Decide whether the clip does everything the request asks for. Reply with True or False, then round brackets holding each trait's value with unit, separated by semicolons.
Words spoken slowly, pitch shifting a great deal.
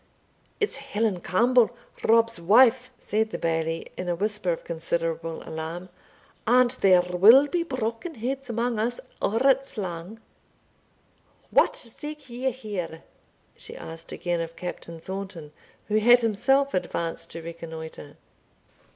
True (130 wpm; 6.5 semitones)